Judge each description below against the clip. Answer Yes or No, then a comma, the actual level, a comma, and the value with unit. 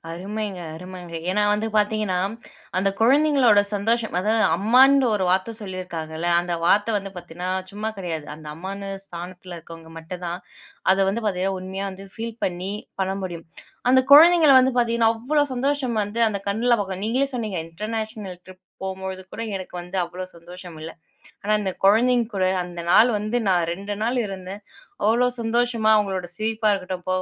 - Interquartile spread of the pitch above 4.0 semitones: No, average, 3.7 semitones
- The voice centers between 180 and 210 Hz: Yes, high, 195 Hz